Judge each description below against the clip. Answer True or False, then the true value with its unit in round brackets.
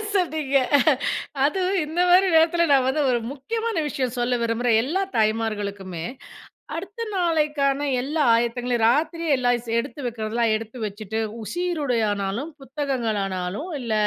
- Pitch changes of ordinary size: False (6.0 semitones)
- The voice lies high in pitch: True (255 Hz)